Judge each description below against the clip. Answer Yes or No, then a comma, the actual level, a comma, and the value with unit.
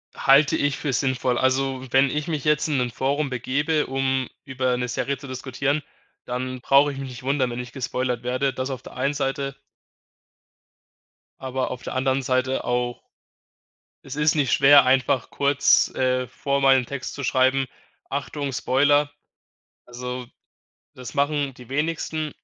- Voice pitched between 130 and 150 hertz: Yes, low, 135 Hz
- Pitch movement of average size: No, narrow, 1.7 semitones